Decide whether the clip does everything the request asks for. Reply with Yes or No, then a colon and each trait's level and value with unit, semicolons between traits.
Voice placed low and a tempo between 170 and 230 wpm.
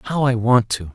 No: low, 120 Hz; fast, 255 wpm